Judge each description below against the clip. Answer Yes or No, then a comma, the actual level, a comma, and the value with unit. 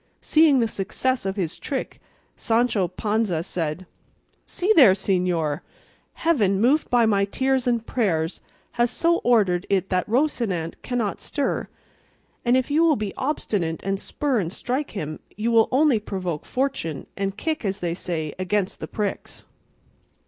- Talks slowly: No, average, 150 wpm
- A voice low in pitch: No, high, 210 Hz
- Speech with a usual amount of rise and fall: No, wide, 5.7 semitones